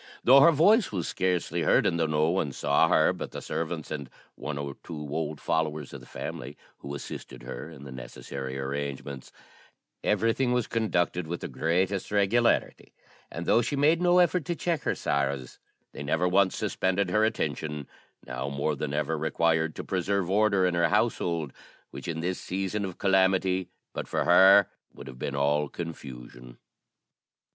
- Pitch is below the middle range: Yes, very low, 85 Hz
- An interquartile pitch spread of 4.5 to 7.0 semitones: Yes, average, 5.2 semitones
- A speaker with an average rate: Yes, average, 170 wpm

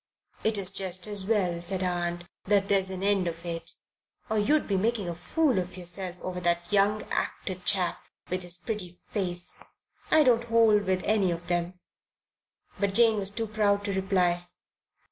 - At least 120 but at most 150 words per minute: No, average, 175 wpm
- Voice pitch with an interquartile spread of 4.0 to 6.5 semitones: No, average, 2.8 semitones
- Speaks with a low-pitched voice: No, high, 190 Hz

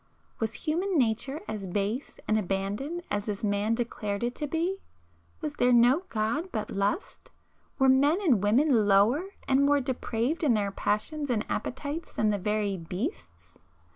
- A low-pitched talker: No, high, 235 Hz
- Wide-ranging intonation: Yes, wide, 5.9 semitones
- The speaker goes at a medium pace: Yes, average, 160 wpm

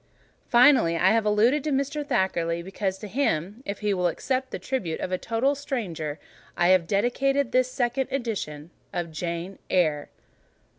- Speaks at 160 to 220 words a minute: No, average, 150 wpm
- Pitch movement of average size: No, wide, 6.8 semitones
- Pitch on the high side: Yes, high, 205 Hz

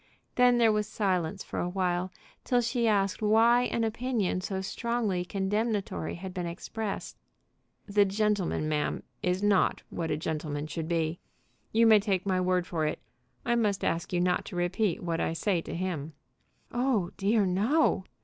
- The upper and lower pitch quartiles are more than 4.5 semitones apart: No, average, 3.8 semitones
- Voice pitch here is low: No, high, 190 Hz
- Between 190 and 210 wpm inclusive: No, average, 165 wpm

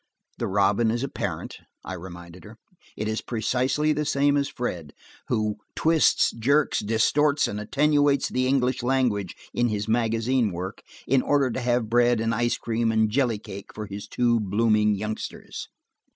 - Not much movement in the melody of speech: No, average, 3.6 semitones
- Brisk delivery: No, average, 165 wpm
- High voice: No, low, 115 Hz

